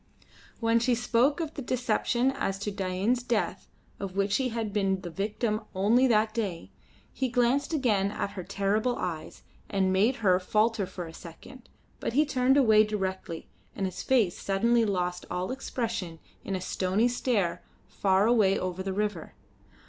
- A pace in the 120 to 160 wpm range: No, average, 170 wpm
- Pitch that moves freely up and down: No, average, 4.2 semitones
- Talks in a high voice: Yes, high, 210 Hz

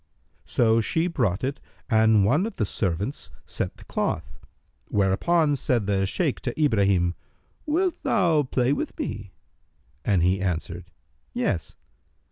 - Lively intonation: Yes, wide, 7.3 semitones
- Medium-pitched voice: No, low, 110 Hz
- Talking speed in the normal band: No, slow, 130 wpm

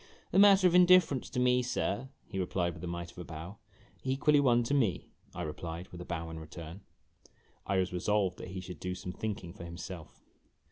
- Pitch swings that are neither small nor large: No, wide, 6.4 semitones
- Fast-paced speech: Yes, fast, 215 wpm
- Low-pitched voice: Yes, very low, 95 Hz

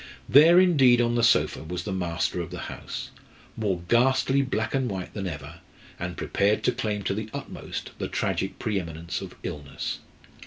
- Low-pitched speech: Yes, low, 105 Hz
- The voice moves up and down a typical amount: No, wide, 5.7 semitones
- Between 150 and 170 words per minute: No, average, 180 wpm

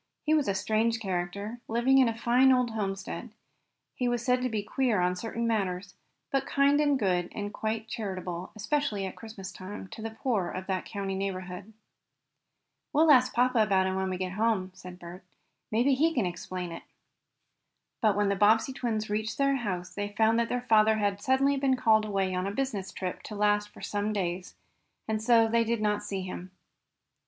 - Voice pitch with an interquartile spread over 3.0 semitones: Yes, average, 3.8 semitones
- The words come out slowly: No, average, 195 wpm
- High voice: Yes, high, 215 Hz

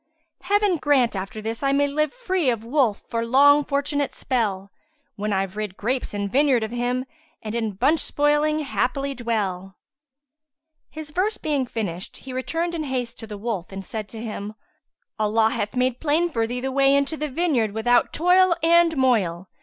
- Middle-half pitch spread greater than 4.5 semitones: Yes, average, 5.2 semitones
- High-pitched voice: Yes, very high, 255 Hz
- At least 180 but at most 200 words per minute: Yes, average, 185 wpm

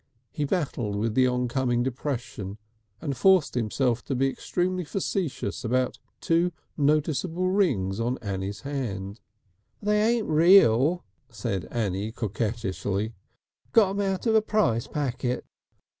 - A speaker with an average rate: No, slow, 125 wpm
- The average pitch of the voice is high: No, low, 130 Hz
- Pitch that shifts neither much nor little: No, wide, 7.6 semitones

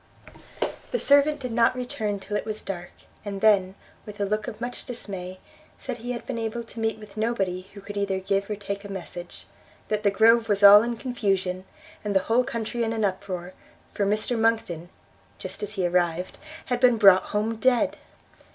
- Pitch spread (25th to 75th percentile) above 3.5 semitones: No, average, 3.0 semitones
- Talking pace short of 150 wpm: No, average, 195 wpm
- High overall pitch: Yes, high, 210 Hz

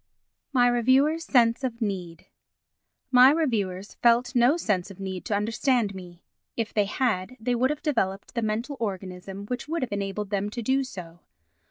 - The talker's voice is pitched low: No, high, 225 Hz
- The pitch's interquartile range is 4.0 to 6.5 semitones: Yes, average, 4.6 semitones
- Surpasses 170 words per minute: No, average, 165 wpm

